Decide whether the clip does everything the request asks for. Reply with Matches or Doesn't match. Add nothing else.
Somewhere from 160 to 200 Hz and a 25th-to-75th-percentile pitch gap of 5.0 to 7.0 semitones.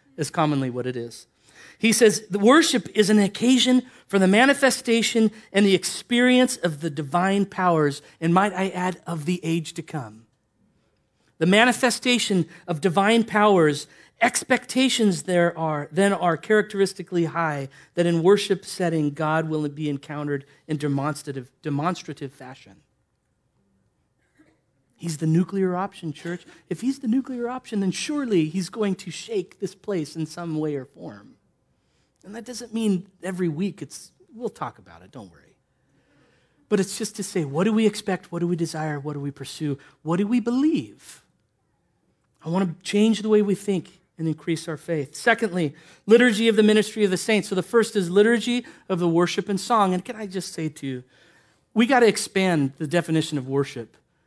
Matches